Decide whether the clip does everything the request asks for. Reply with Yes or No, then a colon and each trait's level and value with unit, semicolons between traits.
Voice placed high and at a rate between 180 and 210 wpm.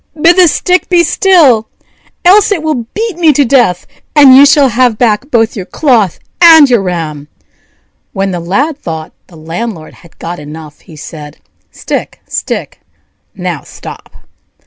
No: high, 235 Hz; average, 155 wpm